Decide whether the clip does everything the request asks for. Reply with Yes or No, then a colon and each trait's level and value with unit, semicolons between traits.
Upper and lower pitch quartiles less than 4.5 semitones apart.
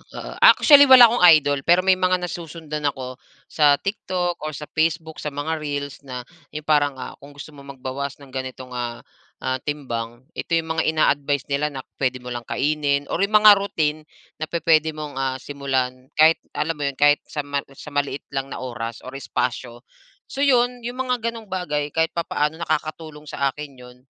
Yes: average, 3.4 semitones